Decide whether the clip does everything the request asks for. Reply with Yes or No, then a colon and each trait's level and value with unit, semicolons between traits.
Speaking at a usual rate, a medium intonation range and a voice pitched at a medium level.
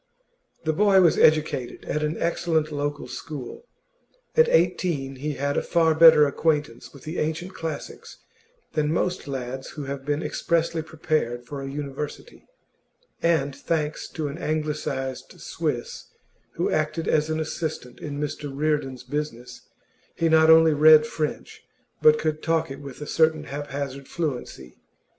No: average, 145 wpm; narrow, 2.3 semitones; medium, 150 Hz